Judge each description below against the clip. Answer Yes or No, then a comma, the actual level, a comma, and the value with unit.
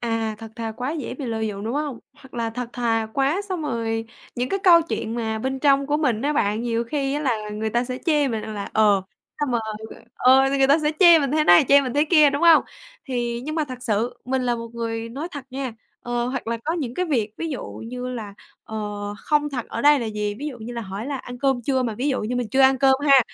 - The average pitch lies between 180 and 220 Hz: No, very high, 250 Hz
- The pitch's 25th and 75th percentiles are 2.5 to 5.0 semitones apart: Yes, average, 3.8 semitones